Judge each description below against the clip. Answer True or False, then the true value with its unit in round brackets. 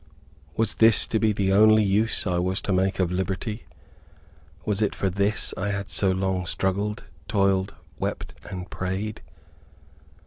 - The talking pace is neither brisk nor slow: True (150 wpm)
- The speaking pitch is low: True (100 Hz)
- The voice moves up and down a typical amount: False (2.0 semitones)